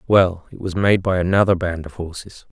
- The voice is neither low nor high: No, very low, 90 Hz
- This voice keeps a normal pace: No, fast, 210 wpm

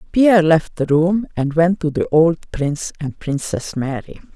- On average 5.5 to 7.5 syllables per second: No, 4.5 syllables/s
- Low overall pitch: No, medium, 160 Hz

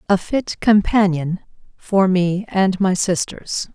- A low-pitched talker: No, high, 190 Hz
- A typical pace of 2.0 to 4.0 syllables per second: Yes, 3.6 syllables/s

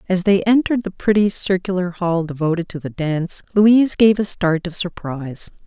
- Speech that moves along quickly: No, average, 180 wpm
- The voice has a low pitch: No, medium, 185 Hz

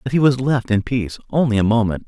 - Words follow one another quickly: Yes, fast, 260 wpm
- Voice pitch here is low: Yes, low, 120 Hz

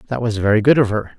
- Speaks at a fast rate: Yes, fast, 305 wpm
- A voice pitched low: Yes, low, 110 Hz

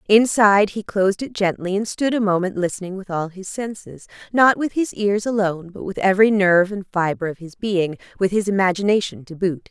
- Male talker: No, female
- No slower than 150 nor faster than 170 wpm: No, average, 190 wpm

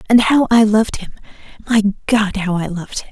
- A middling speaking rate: No, fast, 210 wpm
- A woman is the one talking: Yes, female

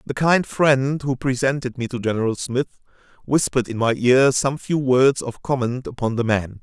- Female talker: No, male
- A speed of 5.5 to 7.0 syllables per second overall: No, 4.9 syllables/s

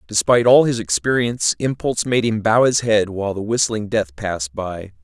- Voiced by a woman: No, male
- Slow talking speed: No, average, 190 wpm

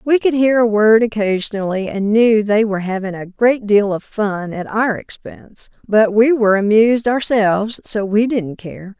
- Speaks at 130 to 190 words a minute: Yes, average, 185 wpm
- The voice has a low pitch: No, high, 215 Hz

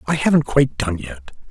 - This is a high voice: No, low, 125 Hz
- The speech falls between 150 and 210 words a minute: Yes, average, 200 wpm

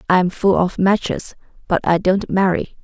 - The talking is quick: No, average, 190 wpm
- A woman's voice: Yes, female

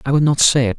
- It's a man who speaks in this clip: Yes, male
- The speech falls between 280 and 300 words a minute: No, fast, 385 wpm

